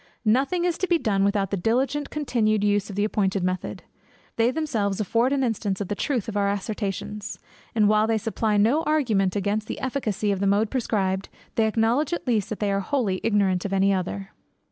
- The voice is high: Yes, high, 210 Hz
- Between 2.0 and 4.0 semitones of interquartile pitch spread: Yes, average, 3.3 semitones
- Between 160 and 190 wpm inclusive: No, fast, 205 wpm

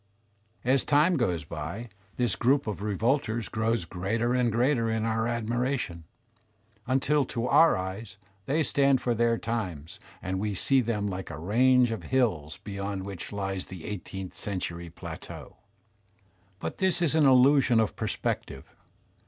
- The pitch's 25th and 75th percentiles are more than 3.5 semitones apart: Yes, average, 4.8 semitones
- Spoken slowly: No, average, 150 wpm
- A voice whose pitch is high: No, low, 115 Hz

